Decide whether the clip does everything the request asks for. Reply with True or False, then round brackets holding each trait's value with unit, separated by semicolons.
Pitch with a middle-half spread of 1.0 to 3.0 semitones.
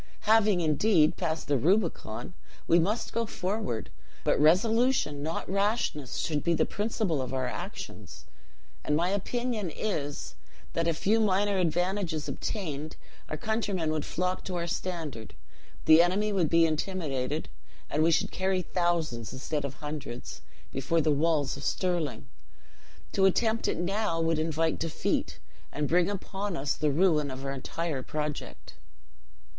False (4.3 semitones)